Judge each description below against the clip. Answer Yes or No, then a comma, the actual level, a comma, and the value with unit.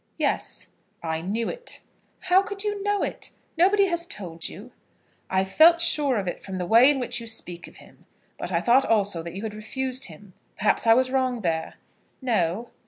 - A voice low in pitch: No, high, 230 Hz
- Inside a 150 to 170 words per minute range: No, average, 195 wpm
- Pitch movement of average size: No, wide, 8.4 semitones